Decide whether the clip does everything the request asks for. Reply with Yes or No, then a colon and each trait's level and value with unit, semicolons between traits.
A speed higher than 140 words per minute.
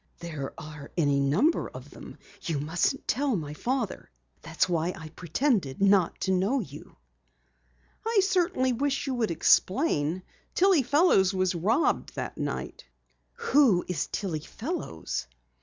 No: slow, 135 wpm